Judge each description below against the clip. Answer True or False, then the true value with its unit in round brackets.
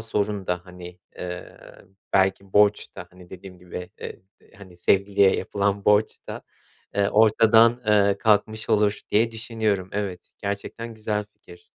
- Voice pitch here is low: True (100 Hz)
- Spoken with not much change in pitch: True (2.3 semitones)